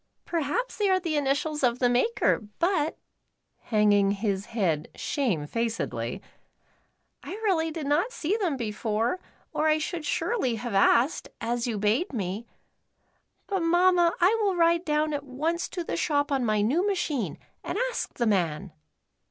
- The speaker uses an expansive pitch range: Yes, wide, 7.3 semitones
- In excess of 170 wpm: No, average, 155 wpm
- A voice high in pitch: Yes, very high, 285 Hz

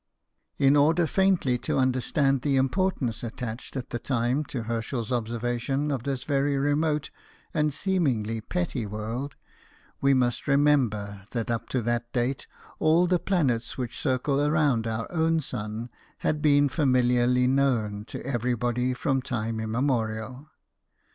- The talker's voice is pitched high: No, low, 130 Hz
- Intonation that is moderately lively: Yes, average, 3.6 semitones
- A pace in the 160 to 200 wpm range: No, slow, 135 wpm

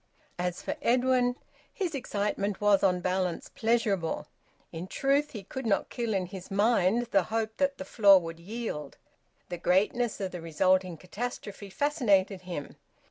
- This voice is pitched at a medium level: No, high, 200 Hz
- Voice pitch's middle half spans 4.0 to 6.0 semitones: Yes, average, 4.6 semitones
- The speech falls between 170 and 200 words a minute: No, average, 150 wpm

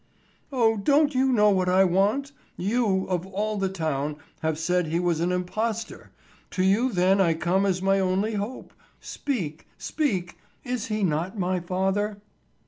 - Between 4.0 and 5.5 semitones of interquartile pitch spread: No, average, 3.2 semitones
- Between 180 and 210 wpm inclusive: No, average, 165 wpm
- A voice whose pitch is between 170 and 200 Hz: Yes, high, 190 Hz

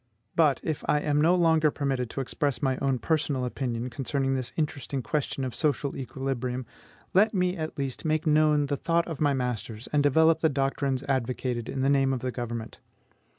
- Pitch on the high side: No, medium, 140 Hz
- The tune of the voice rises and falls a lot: No, average, 3.1 semitones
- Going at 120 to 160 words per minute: No, average, 190 wpm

